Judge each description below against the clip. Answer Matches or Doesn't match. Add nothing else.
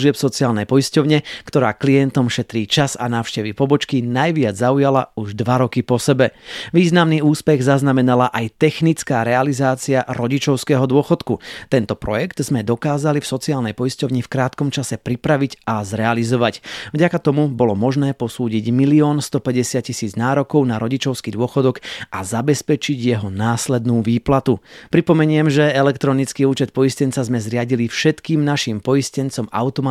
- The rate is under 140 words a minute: Matches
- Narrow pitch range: Doesn't match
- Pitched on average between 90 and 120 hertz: Doesn't match